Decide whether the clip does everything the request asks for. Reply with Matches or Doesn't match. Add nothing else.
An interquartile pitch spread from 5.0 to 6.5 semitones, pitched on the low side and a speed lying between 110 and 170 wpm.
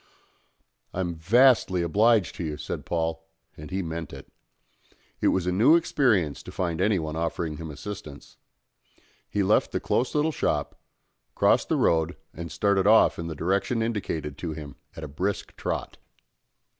Doesn't match